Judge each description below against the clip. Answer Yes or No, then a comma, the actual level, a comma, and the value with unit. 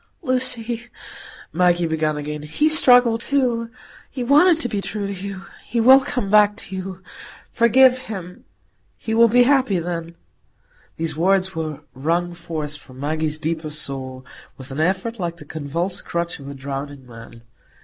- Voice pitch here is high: No, medium, 175 Hz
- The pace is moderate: Yes, average, 155 wpm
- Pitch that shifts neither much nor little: No, wide, 7.3 semitones